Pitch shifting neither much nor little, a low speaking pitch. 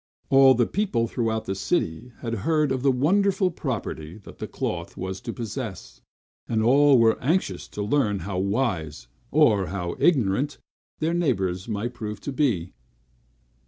No: wide, 6.4 semitones; low, 115 Hz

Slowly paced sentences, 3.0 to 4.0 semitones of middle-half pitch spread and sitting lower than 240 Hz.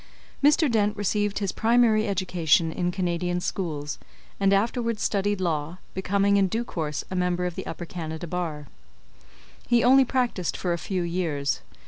No: average, 155 wpm; average, 3.5 semitones; medium, 185 Hz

